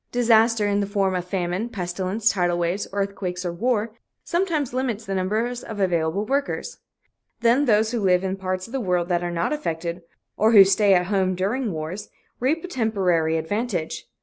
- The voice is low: No, high, 200 Hz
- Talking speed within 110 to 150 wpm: No, average, 180 wpm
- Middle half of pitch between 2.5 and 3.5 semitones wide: No, average, 4.2 semitones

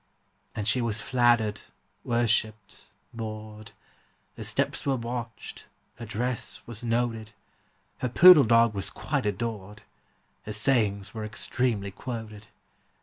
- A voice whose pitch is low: Yes, low, 115 Hz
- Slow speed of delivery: Yes, slow, 115 wpm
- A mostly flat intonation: Yes, narrow, 2.1 semitones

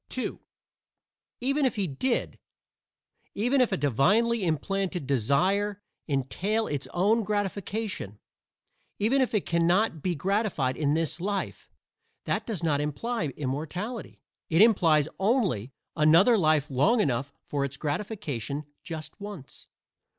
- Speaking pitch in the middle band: Yes, medium, 180 Hz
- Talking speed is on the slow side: Yes, slow, 120 wpm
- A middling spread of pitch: No, wide, 6.6 semitones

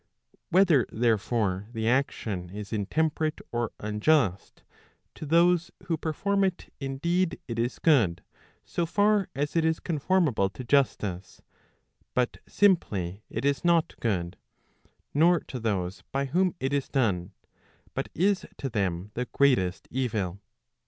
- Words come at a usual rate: No, slow, 130 wpm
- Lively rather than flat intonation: Yes, wide, 7.8 semitones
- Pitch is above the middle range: No, low, 130 Hz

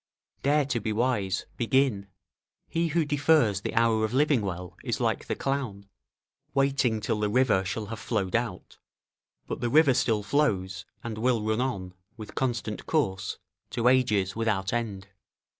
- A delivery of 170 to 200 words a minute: No, average, 160 wpm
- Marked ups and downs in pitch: No, average, 4.5 semitones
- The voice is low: Yes, low, 115 Hz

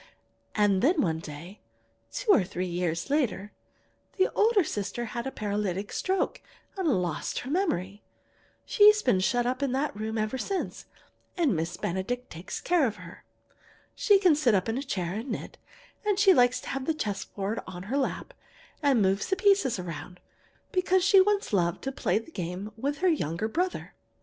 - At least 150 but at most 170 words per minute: No, average, 180 wpm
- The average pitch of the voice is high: Yes, high, 235 Hz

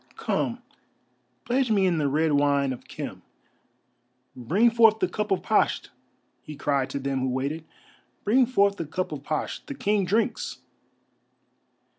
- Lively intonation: Yes, wide, 7.2 semitones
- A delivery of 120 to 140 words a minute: No, average, 150 wpm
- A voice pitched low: No, medium, 165 Hz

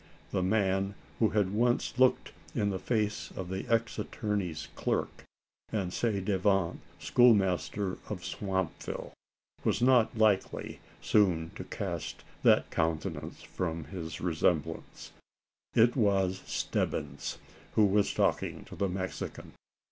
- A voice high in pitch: No, very low, 95 Hz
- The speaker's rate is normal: No, slow, 120 wpm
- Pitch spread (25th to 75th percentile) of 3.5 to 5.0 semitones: No, average, 2.8 semitones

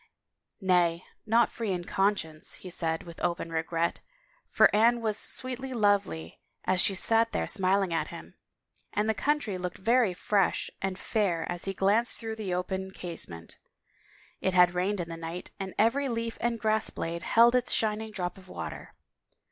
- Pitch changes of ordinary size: Yes, average, 4.0 semitones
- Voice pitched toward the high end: Yes, high, 195 Hz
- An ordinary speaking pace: Yes, average, 180 wpm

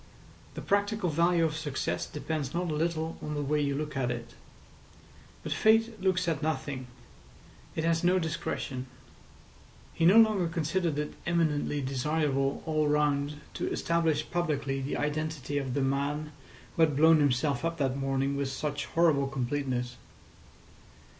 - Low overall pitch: No, medium, 150 Hz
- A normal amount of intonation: Yes, average, 3.1 semitones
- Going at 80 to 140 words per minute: No, average, 150 wpm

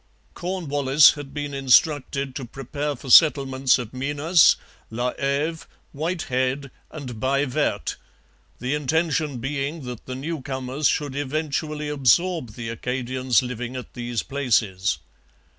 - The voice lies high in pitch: No, low, 135 Hz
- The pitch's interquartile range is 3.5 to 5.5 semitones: No, average, 2.8 semitones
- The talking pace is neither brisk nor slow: No, slow, 120 wpm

